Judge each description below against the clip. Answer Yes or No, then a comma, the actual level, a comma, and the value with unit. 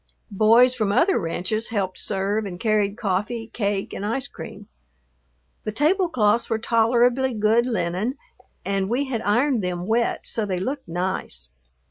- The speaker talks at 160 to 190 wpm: No, average, 145 wpm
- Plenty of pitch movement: No, average, 3.5 semitones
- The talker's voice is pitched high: Yes, high, 215 Hz